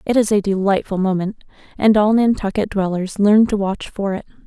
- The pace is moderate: Yes, average, 190 wpm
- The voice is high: Yes, high, 200 Hz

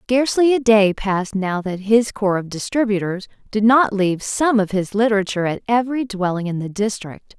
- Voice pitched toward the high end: Yes, high, 210 Hz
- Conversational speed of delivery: Yes, average, 185 wpm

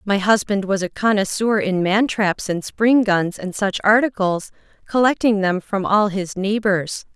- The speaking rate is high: No, average, 170 wpm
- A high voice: Yes, high, 200 Hz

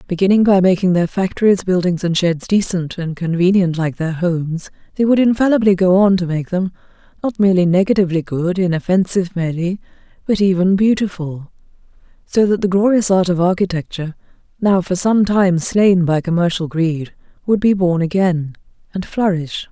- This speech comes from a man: No, female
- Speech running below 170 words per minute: Yes, average, 160 wpm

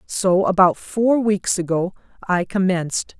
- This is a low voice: No, high, 190 Hz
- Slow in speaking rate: Yes, slow, 130 wpm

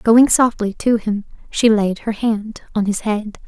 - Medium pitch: No, high, 215 Hz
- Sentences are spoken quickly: No, average, 190 wpm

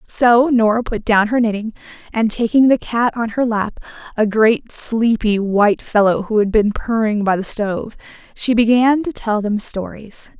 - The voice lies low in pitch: No, high, 220 Hz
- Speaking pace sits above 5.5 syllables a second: No, 4.5 syllables/s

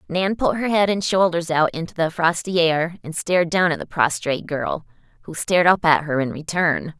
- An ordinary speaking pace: No, fast, 215 wpm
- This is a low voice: No, medium, 165 Hz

